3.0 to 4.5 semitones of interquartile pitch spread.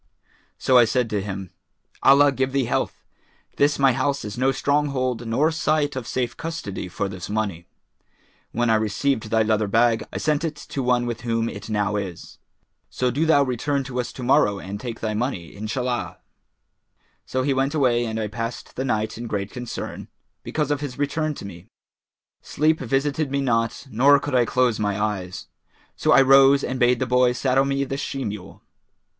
Yes: average, 4.1 semitones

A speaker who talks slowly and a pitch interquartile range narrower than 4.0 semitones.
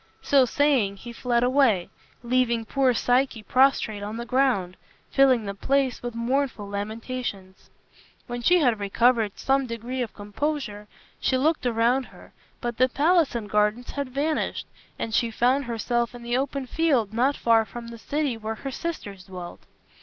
No: average, 160 wpm; average, 3.5 semitones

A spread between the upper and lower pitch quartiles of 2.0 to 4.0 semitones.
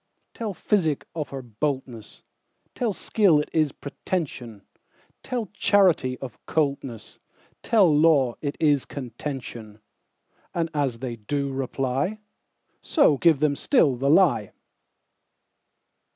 No: average, 4.7 semitones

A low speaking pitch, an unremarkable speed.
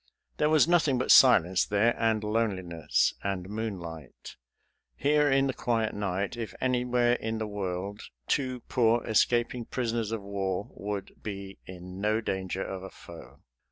Yes: low, 110 Hz; average, 150 wpm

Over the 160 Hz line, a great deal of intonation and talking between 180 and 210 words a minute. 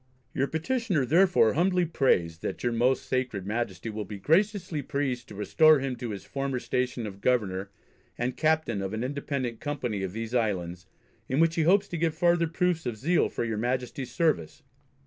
No: low, 130 Hz; wide, 6.4 semitones; average, 185 wpm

